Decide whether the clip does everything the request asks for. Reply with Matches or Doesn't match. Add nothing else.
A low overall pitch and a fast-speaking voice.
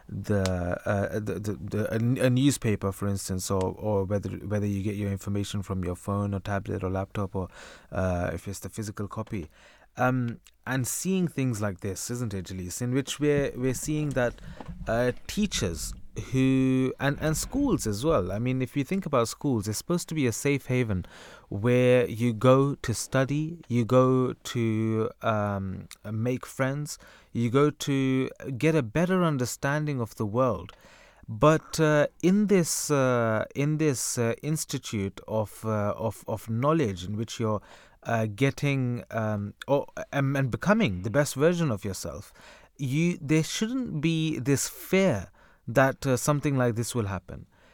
Doesn't match